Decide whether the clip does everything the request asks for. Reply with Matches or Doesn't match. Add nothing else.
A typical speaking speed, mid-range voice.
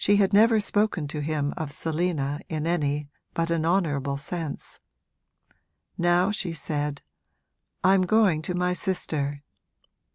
Doesn't match